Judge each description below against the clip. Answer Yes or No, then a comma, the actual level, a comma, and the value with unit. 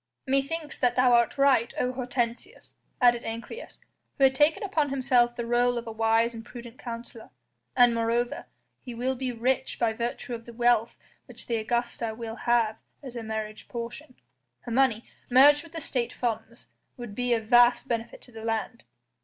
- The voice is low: No, high, 240 Hz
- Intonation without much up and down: Yes, narrow, 1.8 semitones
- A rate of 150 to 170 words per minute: No, average, 180 wpm